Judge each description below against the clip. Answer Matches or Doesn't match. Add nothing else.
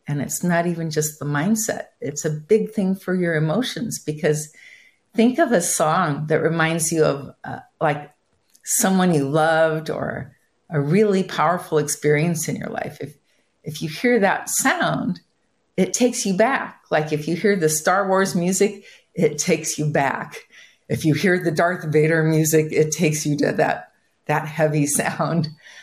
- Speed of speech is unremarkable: Matches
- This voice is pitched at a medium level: Matches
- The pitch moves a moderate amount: Matches